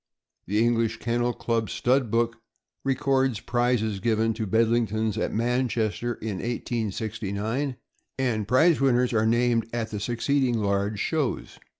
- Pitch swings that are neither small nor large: No, narrow, 2.0 semitones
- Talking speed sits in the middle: No, slow, 125 wpm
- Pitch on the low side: Yes, low, 115 Hz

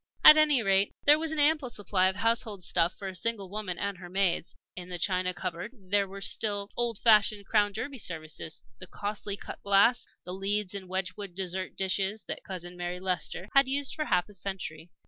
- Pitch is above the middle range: Yes, high, 195 Hz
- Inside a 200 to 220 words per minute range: Yes, fast, 205 wpm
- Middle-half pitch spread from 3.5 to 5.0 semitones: No, average, 2.8 semitones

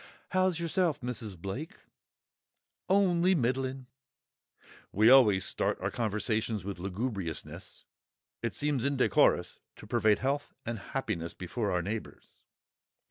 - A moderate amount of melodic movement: No, wide, 5.8 semitones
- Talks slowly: Yes, slow, 110 wpm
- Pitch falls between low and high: No, low, 120 Hz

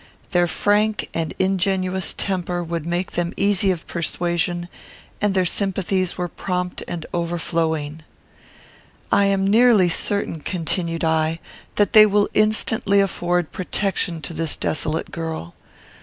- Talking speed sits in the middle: No, slow, 125 wpm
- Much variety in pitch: No, average, 2.8 semitones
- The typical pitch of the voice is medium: Yes, medium, 180 Hz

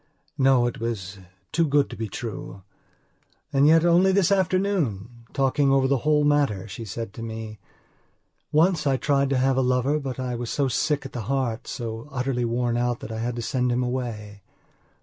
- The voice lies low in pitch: Yes, low, 125 Hz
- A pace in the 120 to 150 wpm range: No, average, 190 wpm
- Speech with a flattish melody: No, average, 3.6 semitones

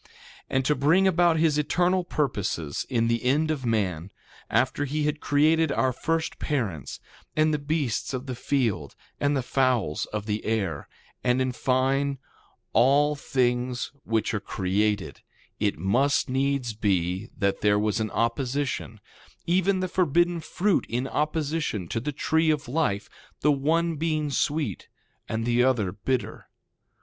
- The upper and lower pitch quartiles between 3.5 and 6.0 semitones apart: Yes, average, 5.3 semitones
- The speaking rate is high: No, average, 150 wpm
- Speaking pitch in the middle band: No, low, 130 Hz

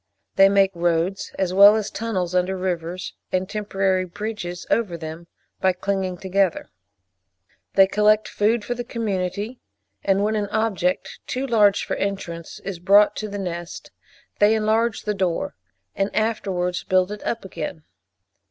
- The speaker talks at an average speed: Yes, average, 150 wpm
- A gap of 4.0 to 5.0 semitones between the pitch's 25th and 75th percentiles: No, average, 2.7 semitones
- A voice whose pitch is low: No, high, 195 Hz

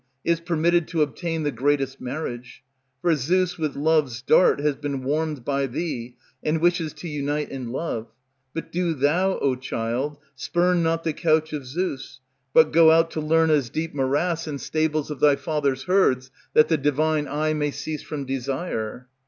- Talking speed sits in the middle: Yes, average, 170 wpm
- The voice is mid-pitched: Yes, medium, 150 Hz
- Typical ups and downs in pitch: Yes, average, 3.1 semitones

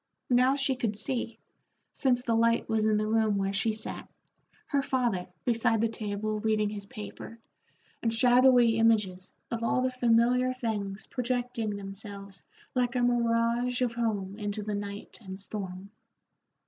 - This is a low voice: No, high, 225 Hz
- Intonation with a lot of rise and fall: No, average, 3.0 semitones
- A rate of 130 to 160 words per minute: Yes, average, 150 wpm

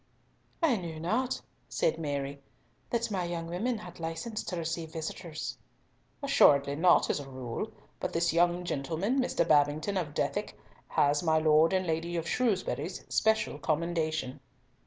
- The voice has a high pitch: No, medium, 165 Hz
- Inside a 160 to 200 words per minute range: No, average, 140 wpm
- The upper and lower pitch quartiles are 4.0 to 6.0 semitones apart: No, average, 3.1 semitones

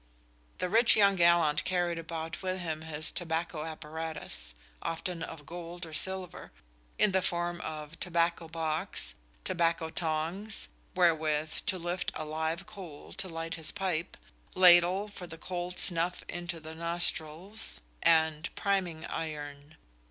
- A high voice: No, medium, 170 Hz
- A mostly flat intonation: Yes, narrow, 2.2 semitones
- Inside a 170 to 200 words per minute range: No, slow, 135 wpm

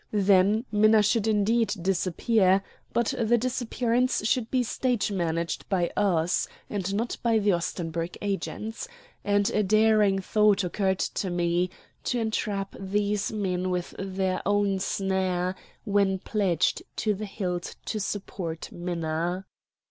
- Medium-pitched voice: No, high, 200 Hz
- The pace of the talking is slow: Yes, slow, 130 wpm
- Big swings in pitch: No, average, 2.9 semitones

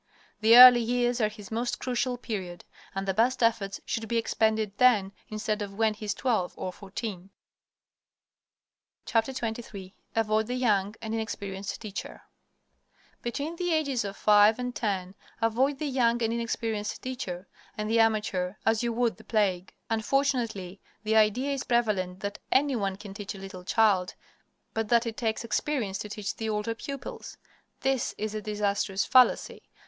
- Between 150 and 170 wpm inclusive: Yes, average, 160 wpm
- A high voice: Yes, high, 220 Hz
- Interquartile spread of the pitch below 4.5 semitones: Yes, average, 2.9 semitones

